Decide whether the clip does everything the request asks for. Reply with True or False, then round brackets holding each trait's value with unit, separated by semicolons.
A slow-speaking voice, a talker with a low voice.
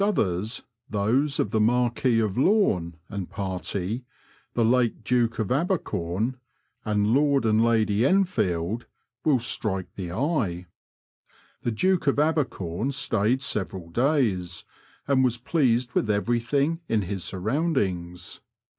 True (125 wpm; 115 Hz)